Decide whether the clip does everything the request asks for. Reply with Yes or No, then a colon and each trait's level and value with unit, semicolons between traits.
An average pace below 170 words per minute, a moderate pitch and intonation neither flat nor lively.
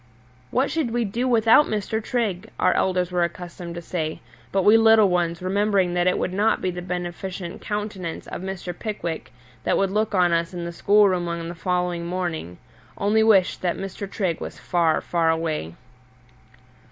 No: average, 175 wpm; medium, 180 Hz; average, 3.3 semitones